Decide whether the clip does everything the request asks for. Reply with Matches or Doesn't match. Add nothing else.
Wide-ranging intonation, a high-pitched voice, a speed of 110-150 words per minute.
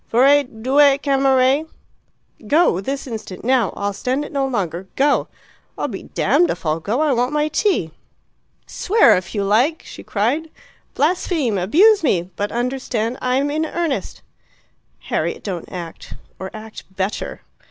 Matches